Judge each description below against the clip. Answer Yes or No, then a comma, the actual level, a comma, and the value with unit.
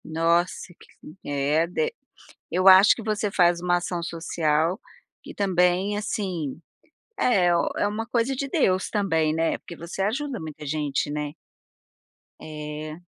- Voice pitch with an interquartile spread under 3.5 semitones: No, average, 4.5 semitones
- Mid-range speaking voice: Yes, medium, 175 Hz